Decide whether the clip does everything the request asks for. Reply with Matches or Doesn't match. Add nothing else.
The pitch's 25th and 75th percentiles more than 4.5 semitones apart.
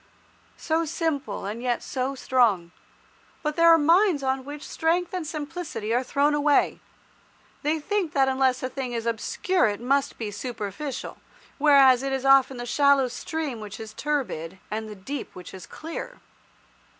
Doesn't match